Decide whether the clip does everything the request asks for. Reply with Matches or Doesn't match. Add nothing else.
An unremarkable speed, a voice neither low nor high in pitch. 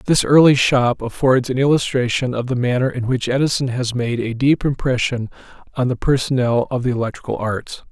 Doesn't match